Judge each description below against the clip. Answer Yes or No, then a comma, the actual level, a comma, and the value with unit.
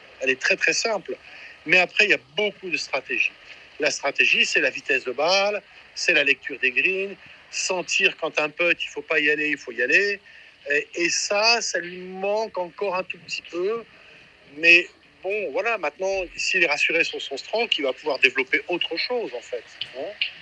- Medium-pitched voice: No, high, 195 Hz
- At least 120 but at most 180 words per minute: No, average, 195 wpm